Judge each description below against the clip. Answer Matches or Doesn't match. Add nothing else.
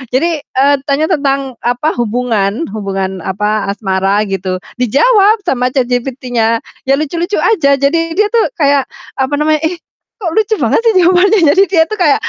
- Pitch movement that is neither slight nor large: Doesn't match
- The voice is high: Matches